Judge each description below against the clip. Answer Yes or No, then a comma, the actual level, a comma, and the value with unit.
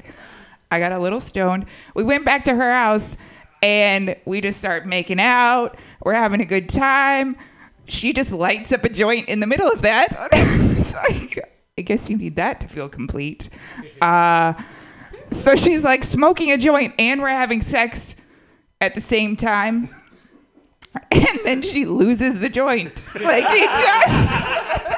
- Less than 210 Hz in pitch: No, high, 220 Hz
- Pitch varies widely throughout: Yes, wide, 5.8 semitones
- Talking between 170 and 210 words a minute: No, average, 160 wpm